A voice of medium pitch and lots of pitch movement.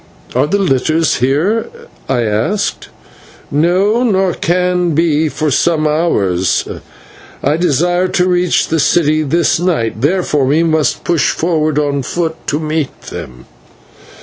No: medium, 160 Hz; average, 3.5 semitones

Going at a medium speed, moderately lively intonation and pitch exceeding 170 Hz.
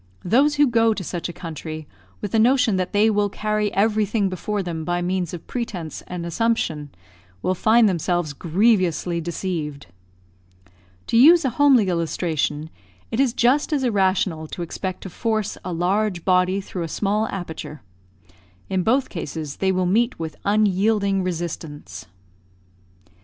Yes: average, 150 wpm; average, 4.3 semitones; high, 190 Hz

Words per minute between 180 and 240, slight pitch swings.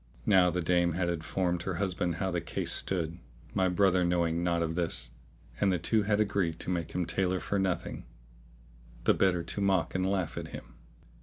Yes: average, 190 wpm; narrow, 1.9 semitones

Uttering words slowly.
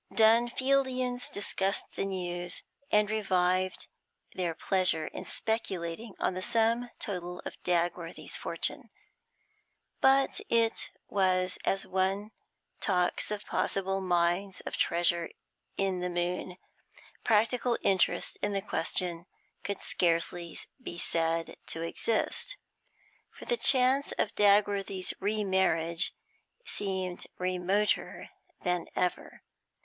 Yes: slow, 105 wpm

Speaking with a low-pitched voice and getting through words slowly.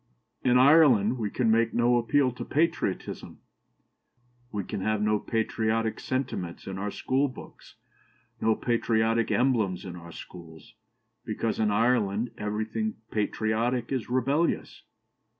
Yes: low, 115 Hz; slow, 120 wpm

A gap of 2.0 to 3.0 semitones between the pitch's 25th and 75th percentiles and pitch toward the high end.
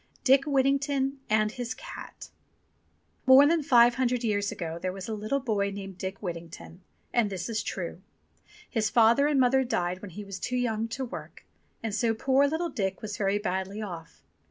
No: average, 5.1 semitones; high, 220 Hz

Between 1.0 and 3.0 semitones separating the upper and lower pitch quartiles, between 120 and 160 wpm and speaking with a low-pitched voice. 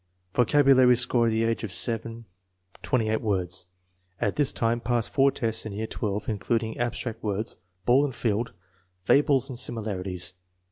Yes: narrow, 2.5 semitones; average, 155 wpm; low, 115 Hz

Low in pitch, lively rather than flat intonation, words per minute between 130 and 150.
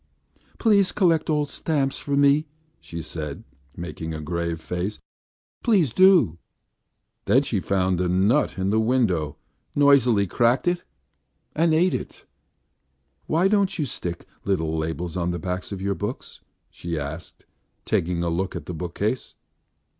Yes: low, 100 Hz; wide, 9.0 semitones; average, 145 wpm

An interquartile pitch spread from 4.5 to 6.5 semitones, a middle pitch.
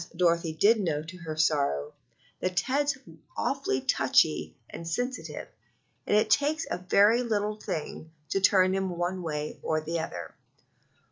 Yes: average, 5.1 semitones; medium, 180 Hz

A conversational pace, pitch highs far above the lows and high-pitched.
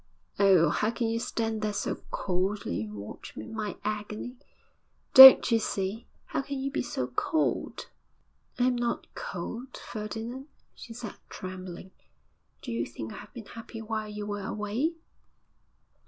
No: average, 150 wpm; average, 3.5 semitones; high, 215 Hz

